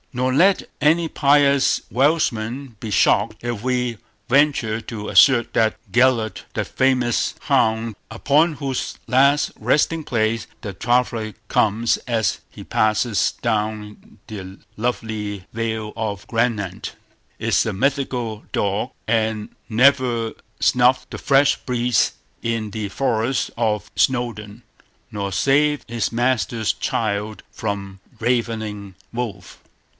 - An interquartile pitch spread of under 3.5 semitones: Yes, average, 3.0 semitones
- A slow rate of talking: Yes, slow, 115 wpm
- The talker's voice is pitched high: No, low, 115 Hz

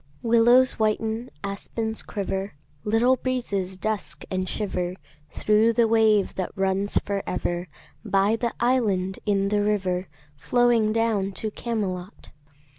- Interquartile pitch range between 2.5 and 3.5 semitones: Yes, average, 3.0 semitones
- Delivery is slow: Yes, slow, 120 wpm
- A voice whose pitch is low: No, high, 210 Hz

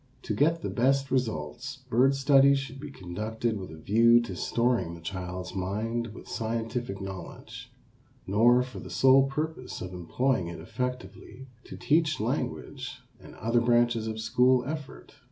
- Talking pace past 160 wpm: No, average, 155 wpm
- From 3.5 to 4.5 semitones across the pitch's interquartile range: Yes, average, 4.2 semitones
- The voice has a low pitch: Yes, low, 120 Hz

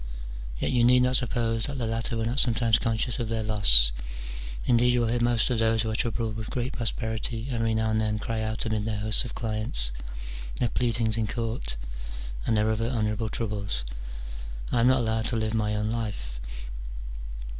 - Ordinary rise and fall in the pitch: No, narrow, 1.6 semitones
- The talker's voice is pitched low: Yes, low, 110 Hz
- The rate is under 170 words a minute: No, average, 200 wpm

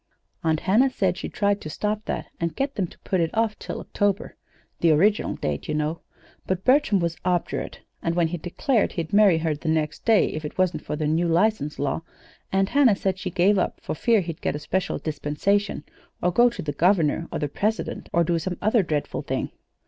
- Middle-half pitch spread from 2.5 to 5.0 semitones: Yes, average, 4.4 semitones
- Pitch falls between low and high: Yes, medium, 180 Hz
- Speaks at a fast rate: Yes, fast, 215 wpm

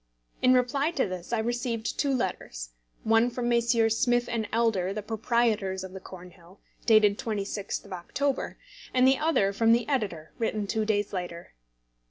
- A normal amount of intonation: Yes, average, 3.7 semitones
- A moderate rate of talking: Yes, average, 165 wpm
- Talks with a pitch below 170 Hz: No, high, 220 Hz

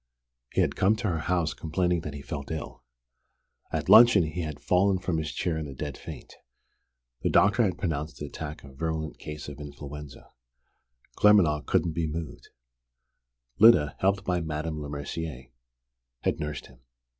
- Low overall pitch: Yes, very low, 80 Hz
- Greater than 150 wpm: Yes, average, 160 wpm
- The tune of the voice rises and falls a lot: No, average, 3.2 semitones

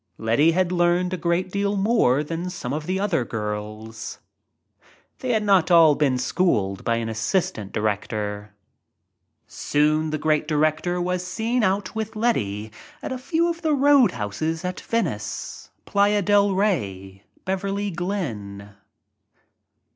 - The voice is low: No, medium, 170 Hz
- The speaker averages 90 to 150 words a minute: Yes, average, 140 wpm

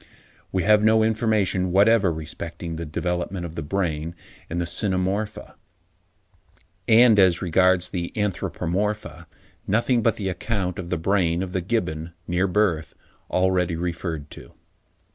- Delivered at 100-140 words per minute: Yes, slow, 135 wpm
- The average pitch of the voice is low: Yes, very low, 90 Hz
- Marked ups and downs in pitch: No, average, 3.4 semitones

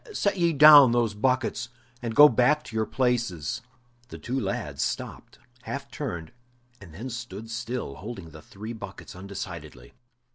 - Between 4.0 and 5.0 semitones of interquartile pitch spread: Yes, average, 4.7 semitones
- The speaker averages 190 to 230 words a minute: No, average, 150 wpm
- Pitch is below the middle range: Yes, low, 115 Hz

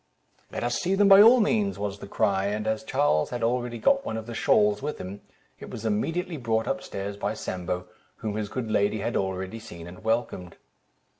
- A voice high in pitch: No, low, 110 Hz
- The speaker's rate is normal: No, fast, 210 wpm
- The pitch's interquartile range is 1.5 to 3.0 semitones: No, average, 3.5 semitones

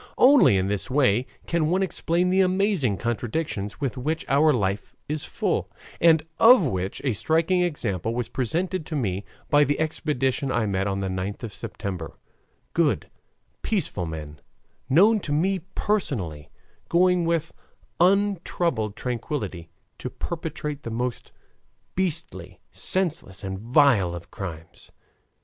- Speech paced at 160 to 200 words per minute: No, slow, 135 wpm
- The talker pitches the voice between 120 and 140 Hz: Yes, low, 135 Hz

